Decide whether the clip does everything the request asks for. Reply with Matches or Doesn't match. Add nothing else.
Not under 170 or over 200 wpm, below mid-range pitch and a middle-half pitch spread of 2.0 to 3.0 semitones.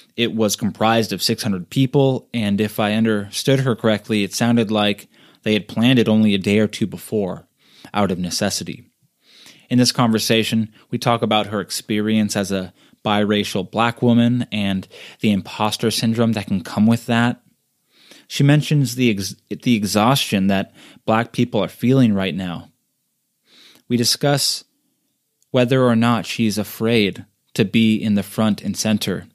Doesn't match